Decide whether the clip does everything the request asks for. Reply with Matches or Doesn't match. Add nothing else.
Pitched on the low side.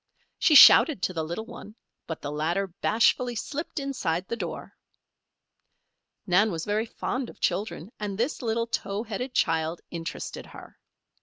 Doesn't match